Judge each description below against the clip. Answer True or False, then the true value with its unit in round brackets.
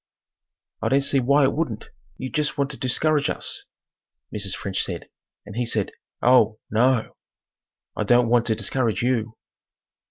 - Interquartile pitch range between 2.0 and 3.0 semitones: False (3.6 semitones)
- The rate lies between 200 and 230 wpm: False (160 wpm)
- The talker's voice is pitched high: False (120 Hz)